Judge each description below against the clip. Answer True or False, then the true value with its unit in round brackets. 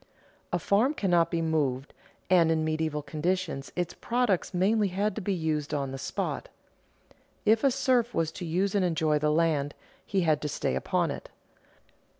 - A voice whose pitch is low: False (170 Hz)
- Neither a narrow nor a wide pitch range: True (4.6 semitones)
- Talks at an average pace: True (170 wpm)